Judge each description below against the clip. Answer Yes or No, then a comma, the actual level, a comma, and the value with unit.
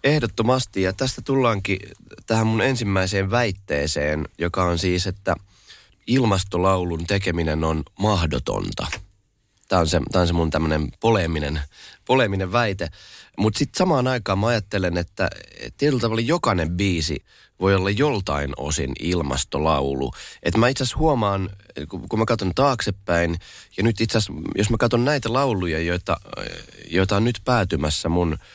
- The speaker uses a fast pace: No, average, 135 wpm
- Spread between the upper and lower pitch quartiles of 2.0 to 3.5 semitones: No, average, 5.3 semitones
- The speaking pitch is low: Yes, very low, 95 Hz